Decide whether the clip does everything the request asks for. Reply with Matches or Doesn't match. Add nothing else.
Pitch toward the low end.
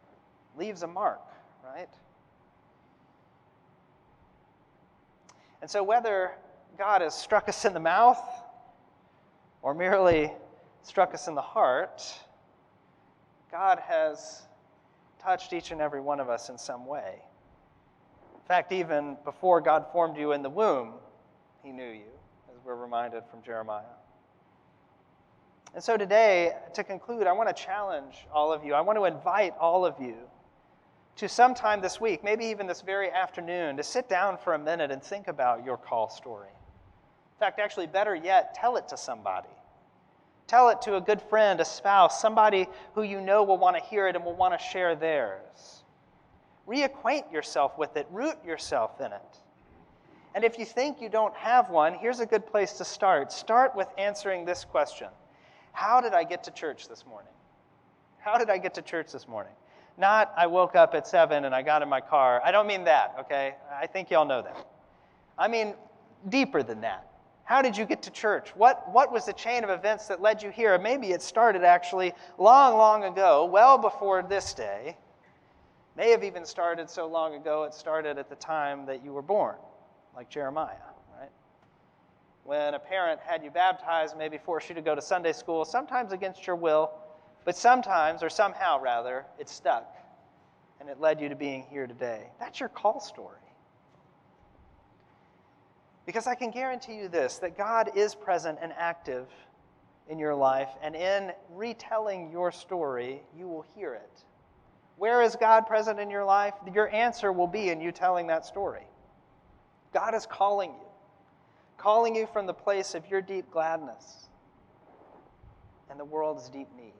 Doesn't match